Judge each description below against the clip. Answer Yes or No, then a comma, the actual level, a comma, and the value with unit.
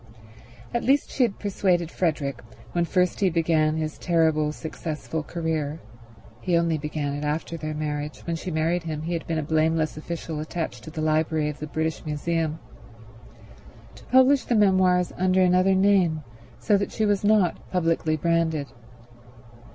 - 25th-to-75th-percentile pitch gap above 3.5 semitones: No, average, 2.7 semitones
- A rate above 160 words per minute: No, average, 155 wpm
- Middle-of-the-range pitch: Yes, medium, 160 Hz